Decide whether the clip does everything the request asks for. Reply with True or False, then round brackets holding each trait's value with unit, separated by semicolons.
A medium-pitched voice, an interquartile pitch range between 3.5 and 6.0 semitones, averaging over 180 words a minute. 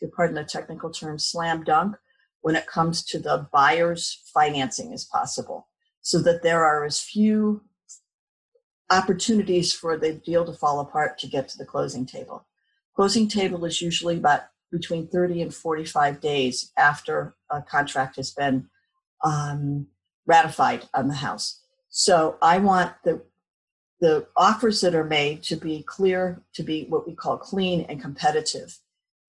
False (170 Hz; 4.7 semitones; 150 wpm)